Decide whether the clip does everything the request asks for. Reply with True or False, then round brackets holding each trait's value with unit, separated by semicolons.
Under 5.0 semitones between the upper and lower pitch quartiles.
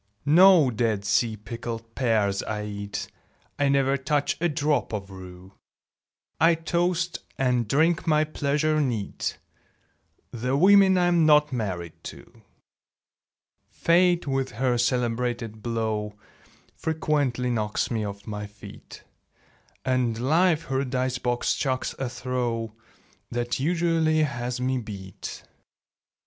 False (5.3 semitones)